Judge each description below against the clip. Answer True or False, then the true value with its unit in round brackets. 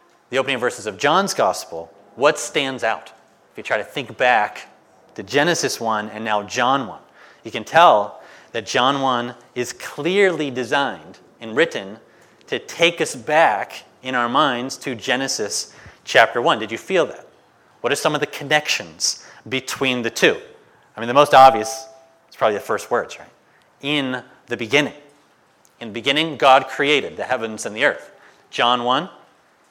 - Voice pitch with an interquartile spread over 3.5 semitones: True (4.5 semitones)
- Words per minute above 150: True (170 wpm)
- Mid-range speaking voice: False (130 Hz)